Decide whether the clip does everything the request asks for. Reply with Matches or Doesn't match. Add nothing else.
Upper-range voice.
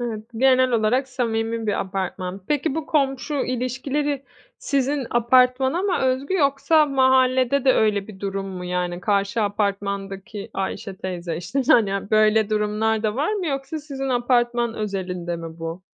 Matches